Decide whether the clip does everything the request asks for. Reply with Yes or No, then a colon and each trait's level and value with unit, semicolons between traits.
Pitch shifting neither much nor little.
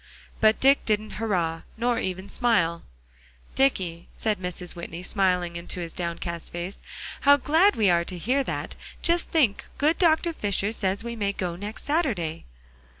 No: wide, 6.0 semitones